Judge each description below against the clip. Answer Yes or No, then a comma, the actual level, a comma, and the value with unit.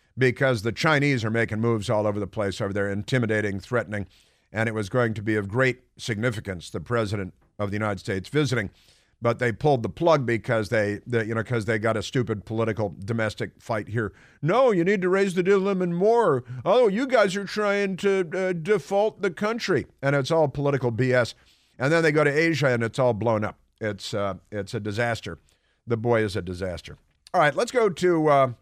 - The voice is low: Yes, low, 120 Hz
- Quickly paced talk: Yes, fast, 210 wpm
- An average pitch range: No, wide, 6.2 semitones